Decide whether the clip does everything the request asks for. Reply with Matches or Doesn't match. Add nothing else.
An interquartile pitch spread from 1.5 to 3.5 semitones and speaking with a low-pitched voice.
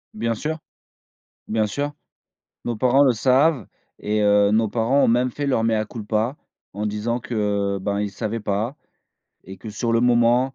Matches